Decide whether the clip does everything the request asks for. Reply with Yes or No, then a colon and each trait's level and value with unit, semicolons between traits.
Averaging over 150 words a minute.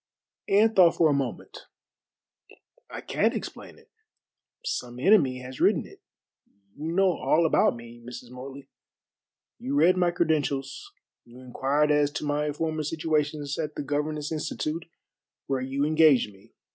No: average, 145 wpm